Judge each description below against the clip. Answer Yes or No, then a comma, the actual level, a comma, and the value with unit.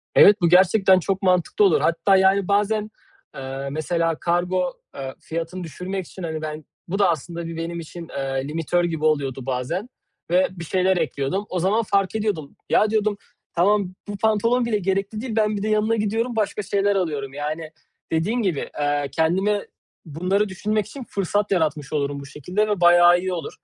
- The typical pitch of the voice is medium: Yes, medium, 180 Hz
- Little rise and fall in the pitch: No, average, 4.2 semitones